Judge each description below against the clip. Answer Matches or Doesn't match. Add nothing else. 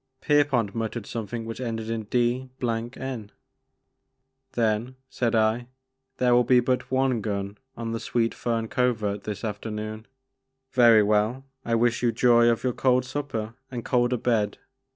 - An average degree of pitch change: Doesn't match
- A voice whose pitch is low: Matches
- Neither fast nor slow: Matches